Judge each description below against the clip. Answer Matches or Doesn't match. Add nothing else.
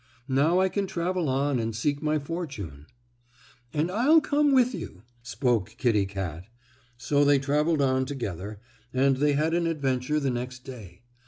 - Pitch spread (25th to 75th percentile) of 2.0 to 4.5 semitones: Doesn't match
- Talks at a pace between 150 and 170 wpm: Matches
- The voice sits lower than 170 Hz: Matches